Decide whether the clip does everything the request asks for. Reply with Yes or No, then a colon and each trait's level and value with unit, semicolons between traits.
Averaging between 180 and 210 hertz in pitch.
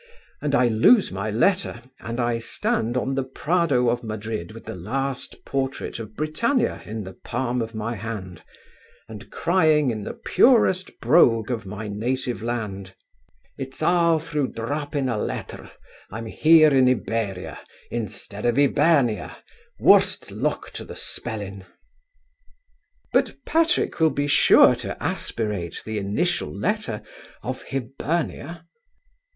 No: low, 120 Hz